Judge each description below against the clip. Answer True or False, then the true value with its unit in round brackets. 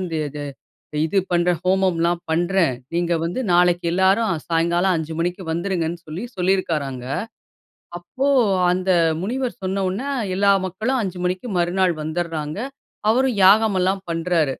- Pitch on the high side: False (180 Hz)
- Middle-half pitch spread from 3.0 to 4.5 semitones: False (2.4 semitones)